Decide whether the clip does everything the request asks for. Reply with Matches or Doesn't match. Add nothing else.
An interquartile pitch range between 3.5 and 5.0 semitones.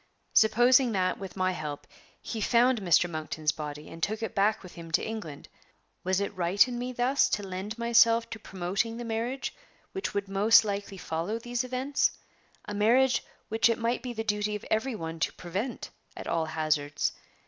Matches